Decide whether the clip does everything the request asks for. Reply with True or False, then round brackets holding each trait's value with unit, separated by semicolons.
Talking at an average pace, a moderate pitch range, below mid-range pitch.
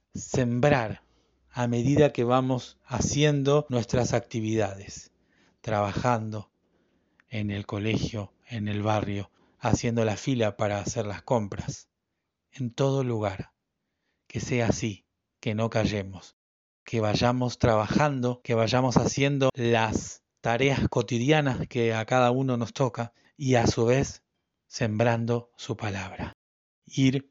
False (120 wpm; 3.5 semitones; 115 Hz)